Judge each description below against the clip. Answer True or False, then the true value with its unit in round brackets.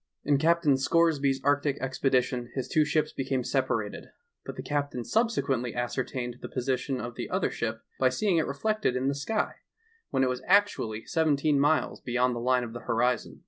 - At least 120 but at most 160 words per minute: False (180 wpm)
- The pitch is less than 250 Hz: True (135 Hz)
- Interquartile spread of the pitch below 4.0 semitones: True (3.2 semitones)